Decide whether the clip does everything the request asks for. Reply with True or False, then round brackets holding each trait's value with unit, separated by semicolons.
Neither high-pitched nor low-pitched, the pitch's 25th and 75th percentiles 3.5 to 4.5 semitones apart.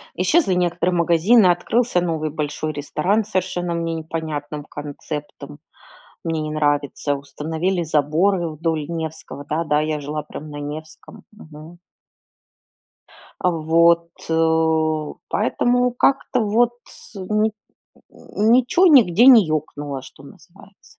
True (165 Hz; 4.0 semitones)